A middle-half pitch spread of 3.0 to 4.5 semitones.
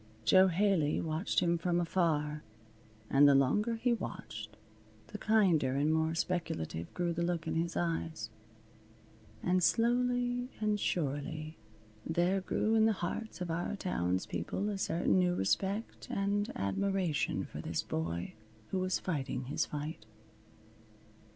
No: average, 5.0 semitones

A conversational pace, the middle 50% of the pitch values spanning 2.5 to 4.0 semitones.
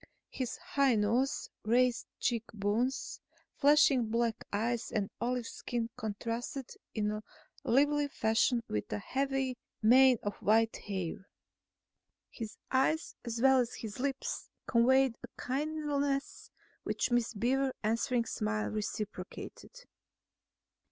No: slow, 110 wpm; average, 3.5 semitones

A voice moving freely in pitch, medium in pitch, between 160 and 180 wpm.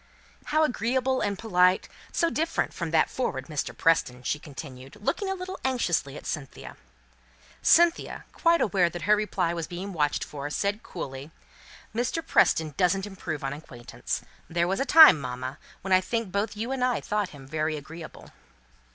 Yes: wide, 7.4 semitones; medium, 180 Hz; average, 170 wpm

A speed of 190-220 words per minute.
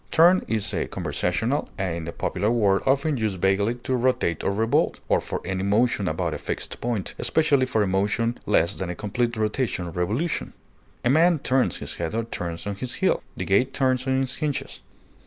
Yes: average, 195 wpm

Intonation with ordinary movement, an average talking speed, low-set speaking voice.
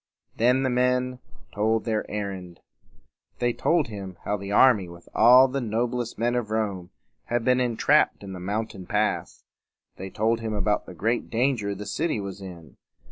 Yes: average, 3.6 semitones; average, 175 wpm; low, 110 Hz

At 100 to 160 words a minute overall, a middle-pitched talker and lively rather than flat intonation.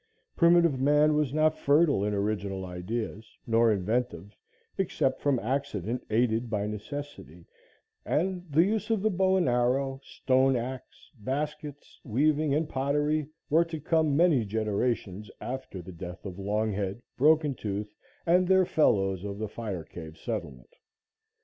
No: average, 140 wpm; low, 125 Hz; wide, 6.6 semitones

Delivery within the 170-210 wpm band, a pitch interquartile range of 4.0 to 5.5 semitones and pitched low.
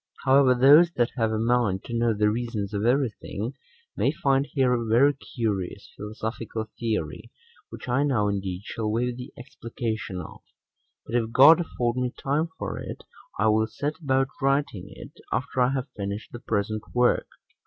No: average, 175 wpm; average, 3.6 semitones; low, 120 Hz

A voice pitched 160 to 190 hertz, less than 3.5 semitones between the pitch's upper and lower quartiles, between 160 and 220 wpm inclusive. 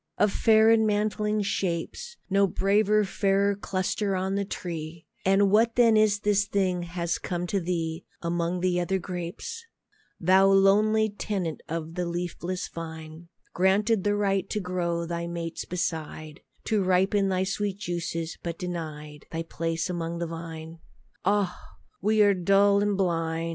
No: medium, 185 Hz; average, 3.1 semitones; average, 150 wpm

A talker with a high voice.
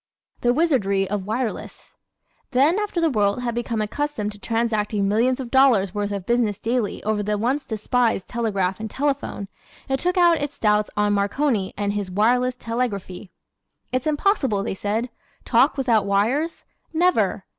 Yes: high, 230 Hz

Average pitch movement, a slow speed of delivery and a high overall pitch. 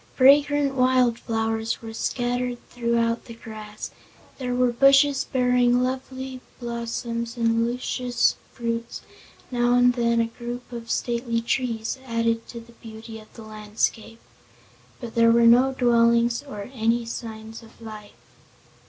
No: narrow, 1.4 semitones; slow, 130 wpm; high, 235 Hz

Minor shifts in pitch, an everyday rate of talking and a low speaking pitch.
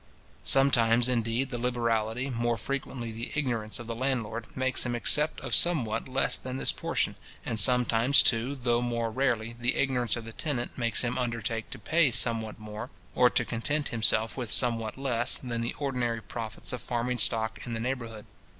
Yes: narrow, 2.1 semitones; average, 175 wpm; low, 120 Hz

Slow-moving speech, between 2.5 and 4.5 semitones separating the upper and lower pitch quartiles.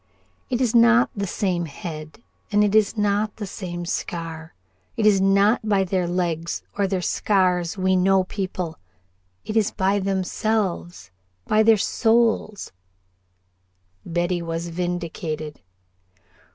Yes: slow, 125 wpm; average, 3.3 semitones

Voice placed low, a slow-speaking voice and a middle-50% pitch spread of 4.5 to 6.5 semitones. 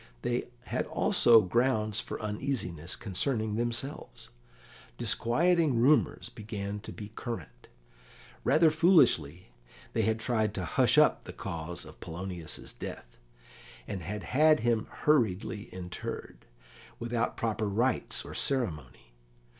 Yes: low, 110 Hz; slow, 115 wpm; average, 5.1 semitones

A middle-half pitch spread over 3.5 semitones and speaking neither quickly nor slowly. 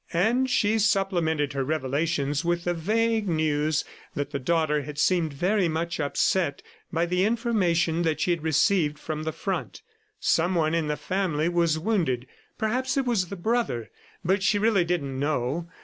Yes: average, 4.4 semitones; average, 165 wpm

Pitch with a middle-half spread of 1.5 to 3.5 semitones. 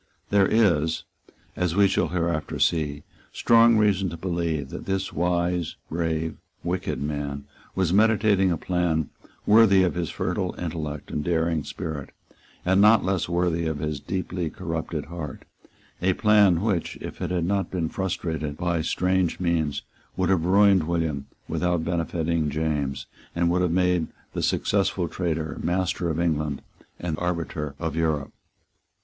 Yes: average, 2.7 semitones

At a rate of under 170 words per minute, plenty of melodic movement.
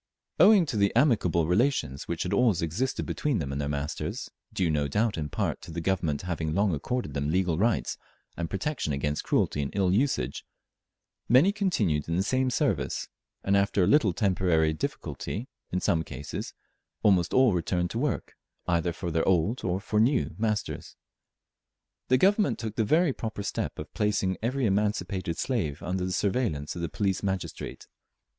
No: average, 175 wpm; wide, 5.8 semitones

